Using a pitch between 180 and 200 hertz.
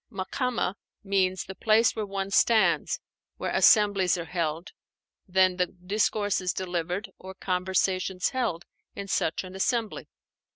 Yes: high, 190 Hz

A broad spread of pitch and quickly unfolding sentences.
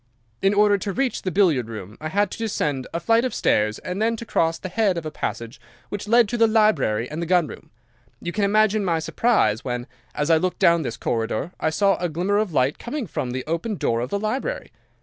Yes: wide, 7.0 semitones; fast, 235 wpm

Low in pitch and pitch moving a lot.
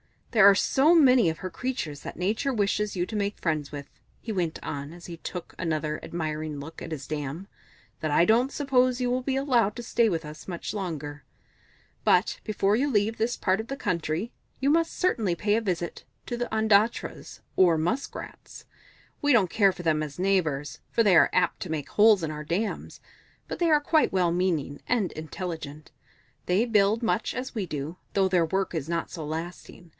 No: medium, 185 Hz; wide, 6.0 semitones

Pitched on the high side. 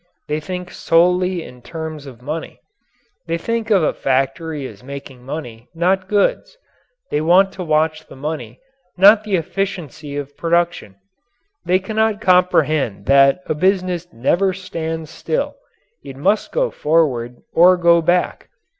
No: medium, 165 Hz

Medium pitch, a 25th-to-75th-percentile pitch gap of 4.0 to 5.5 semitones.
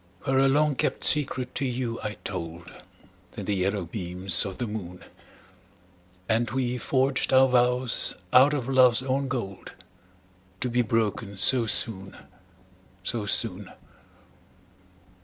No: low, 120 Hz; average, 4.7 semitones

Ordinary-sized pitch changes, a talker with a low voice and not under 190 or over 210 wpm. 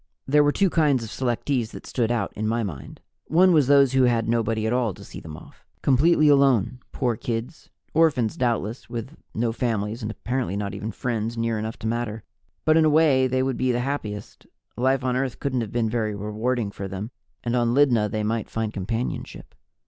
Yes: average, 3.2 semitones; low, 120 Hz; fast, 205 wpm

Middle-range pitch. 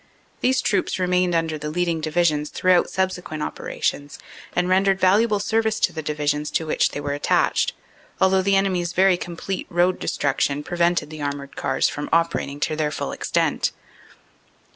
Yes: medium, 175 Hz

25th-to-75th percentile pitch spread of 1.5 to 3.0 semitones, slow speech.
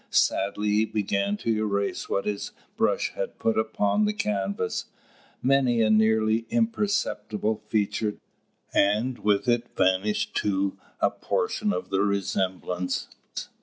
Yes: narrow, 2.4 semitones; slow, 130 wpm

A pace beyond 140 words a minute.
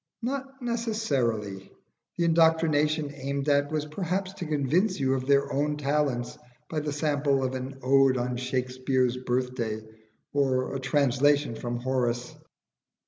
No: slow, 135 wpm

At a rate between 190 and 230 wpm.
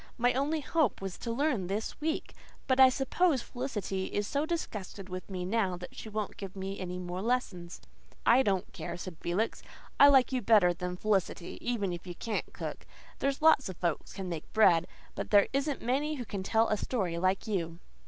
Yes: average, 200 wpm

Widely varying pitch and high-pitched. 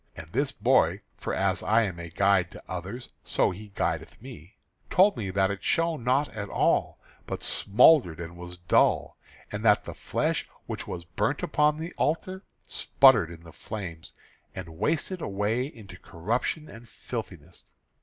No: wide, 7.1 semitones; low, 105 Hz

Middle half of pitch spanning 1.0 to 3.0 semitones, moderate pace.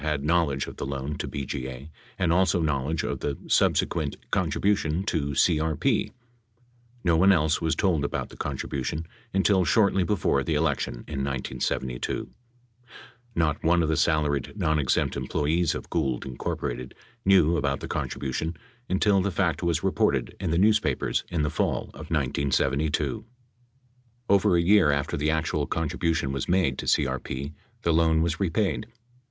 No: average, 3.6 semitones; average, 155 wpm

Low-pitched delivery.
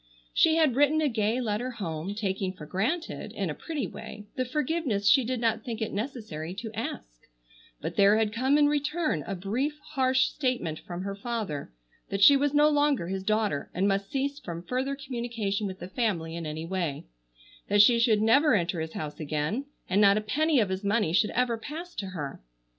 No: high, 220 Hz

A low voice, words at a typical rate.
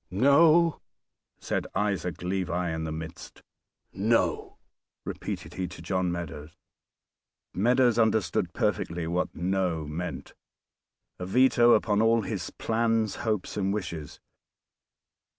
No: very low, 95 Hz; slow, 110 wpm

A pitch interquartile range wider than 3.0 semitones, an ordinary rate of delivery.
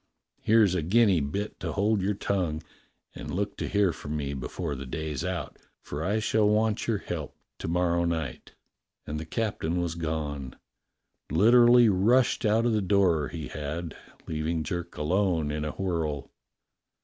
Yes: average, 5.0 semitones; average, 160 wpm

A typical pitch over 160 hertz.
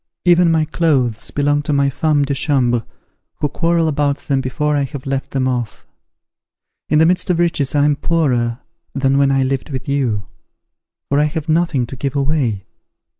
No: medium, 140 Hz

